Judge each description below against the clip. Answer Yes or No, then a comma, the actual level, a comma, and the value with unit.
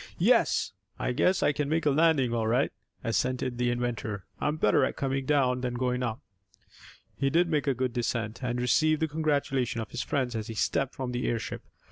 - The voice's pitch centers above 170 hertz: No, low, 130 Hz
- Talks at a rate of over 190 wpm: Yes, average, 200 wpm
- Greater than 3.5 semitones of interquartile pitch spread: No, average, 3.1 semitones